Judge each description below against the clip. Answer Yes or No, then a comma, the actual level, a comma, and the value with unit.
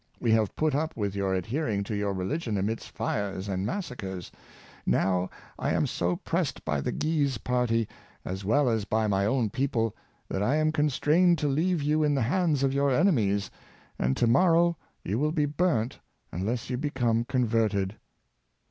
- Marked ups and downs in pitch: Yes, wide, 6.6 semitones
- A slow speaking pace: No, average, 175 wpm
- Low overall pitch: Yes, low, 120 Hz